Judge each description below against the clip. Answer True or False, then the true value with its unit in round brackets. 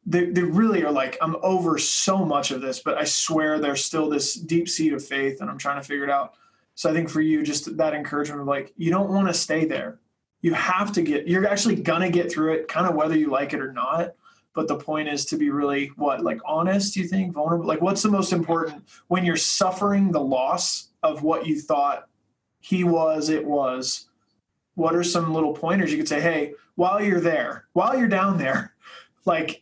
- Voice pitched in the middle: True (160 Hz)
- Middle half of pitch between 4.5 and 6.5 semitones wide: False (3.5 semitones)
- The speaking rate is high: True (225 wpm)